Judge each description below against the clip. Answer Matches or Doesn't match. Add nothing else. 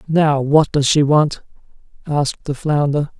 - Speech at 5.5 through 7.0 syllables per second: Doesn't match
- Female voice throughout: Doesn't match